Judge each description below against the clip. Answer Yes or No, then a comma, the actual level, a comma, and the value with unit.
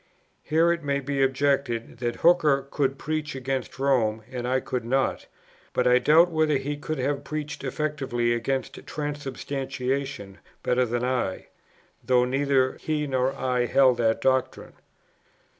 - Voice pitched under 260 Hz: Yes, low, 135 Hz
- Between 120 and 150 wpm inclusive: Yes, average, 140 wpm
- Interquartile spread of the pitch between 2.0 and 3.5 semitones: Yes, narrow, 2.4 semitones